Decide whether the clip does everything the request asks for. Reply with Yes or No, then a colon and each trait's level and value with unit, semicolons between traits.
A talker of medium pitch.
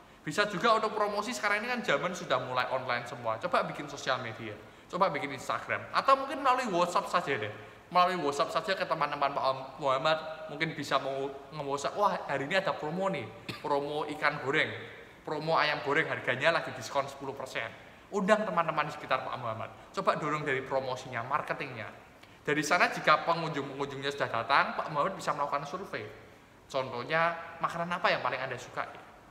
Yes: medium, 145 Hz